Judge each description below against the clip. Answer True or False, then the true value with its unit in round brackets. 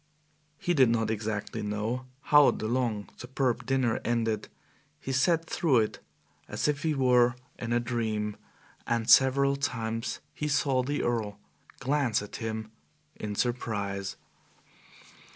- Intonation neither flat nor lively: True (3.4 semitones)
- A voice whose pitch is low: True (120 Hz)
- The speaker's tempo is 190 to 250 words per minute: False (135 wpm)